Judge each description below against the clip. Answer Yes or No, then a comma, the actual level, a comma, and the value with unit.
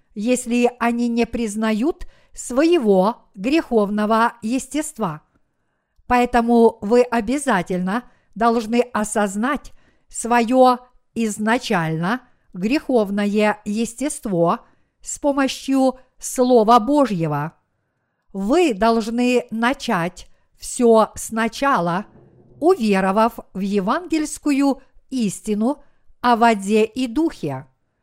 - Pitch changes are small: No, average, 3.5 semitones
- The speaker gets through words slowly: Yes, slow, 70 wpm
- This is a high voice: Yes, high, 235 Hz